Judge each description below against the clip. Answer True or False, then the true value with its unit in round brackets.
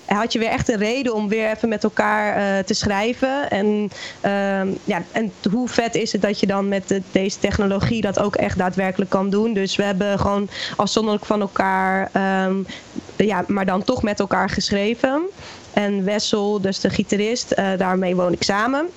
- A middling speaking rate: True (190 wpm)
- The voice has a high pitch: True (205 Hz)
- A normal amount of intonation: False (2.0 semitones)